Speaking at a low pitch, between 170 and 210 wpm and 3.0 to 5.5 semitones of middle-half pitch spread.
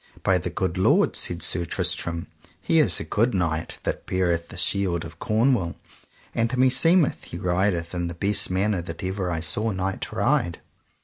Yes: very low, 90 Hz; average, 175 wpm; average, 3.4 semitones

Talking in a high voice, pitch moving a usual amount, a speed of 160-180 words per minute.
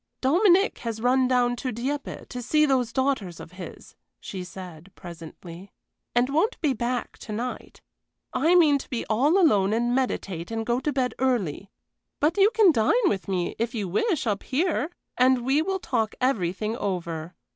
No: high, 245 Hz; wide, 6.2 semitones; average, 175 wpm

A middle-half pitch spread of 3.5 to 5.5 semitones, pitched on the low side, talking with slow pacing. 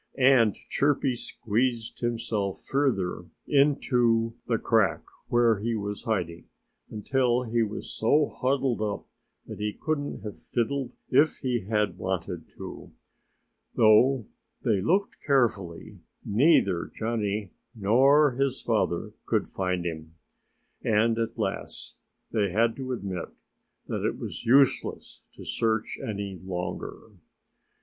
Yes: average, 4.2 semitones; low, 115 Hz; slow, 120 wpm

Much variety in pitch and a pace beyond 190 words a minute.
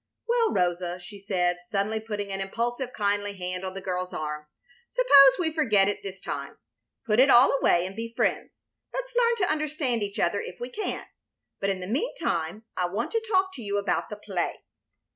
Yes: wide, 6.8 semitones; average, 200 wpm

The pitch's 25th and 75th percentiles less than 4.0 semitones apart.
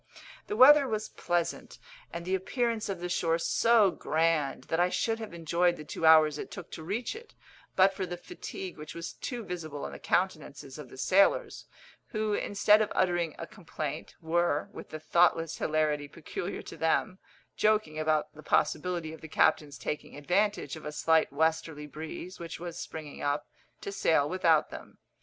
Yes: average, 3.6 semitones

